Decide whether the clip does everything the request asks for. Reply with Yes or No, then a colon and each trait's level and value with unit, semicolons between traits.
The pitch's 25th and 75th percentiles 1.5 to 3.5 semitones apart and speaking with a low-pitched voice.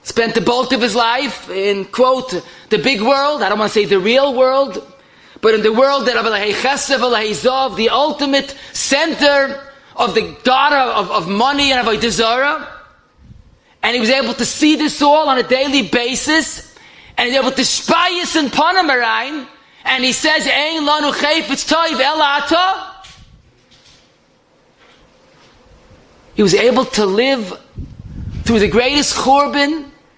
No: average, 3.2 semitones; very high, 265 Hz